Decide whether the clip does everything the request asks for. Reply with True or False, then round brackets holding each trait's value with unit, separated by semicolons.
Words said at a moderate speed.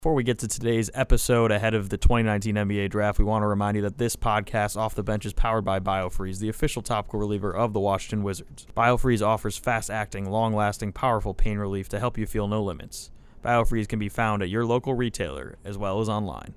False (225 wpm)